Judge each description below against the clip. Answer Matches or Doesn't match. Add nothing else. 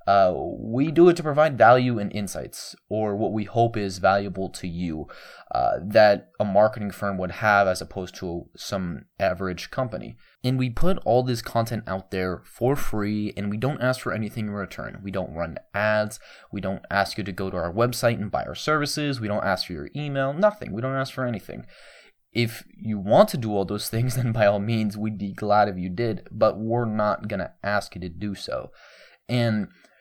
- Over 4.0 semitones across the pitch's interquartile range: Doesn't match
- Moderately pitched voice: Doesn't match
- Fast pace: Matches